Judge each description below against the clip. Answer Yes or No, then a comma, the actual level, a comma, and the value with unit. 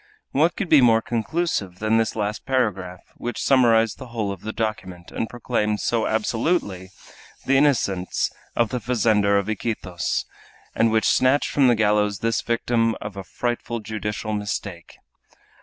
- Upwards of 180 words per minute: No, average, 155 wpm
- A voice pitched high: No, low, 110 Hz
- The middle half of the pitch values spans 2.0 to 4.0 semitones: Yes, average, 2.8 semitones